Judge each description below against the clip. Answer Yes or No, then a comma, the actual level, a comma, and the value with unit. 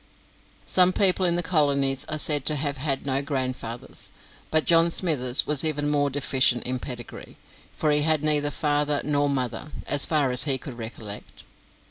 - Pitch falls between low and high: Yes, medium, 145 Hz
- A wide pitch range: No, narrow, 2.6 semitones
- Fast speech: No, average, 170 wpm